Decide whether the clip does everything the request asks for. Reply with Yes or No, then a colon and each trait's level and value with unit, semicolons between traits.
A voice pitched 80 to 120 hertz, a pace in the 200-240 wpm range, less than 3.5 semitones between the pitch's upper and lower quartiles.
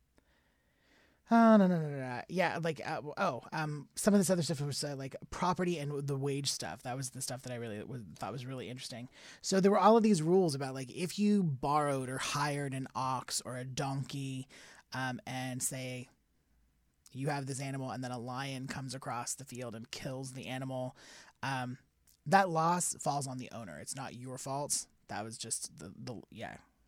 No: low, 135 Hz; fast, 205 wpm; average, 2.9 semitones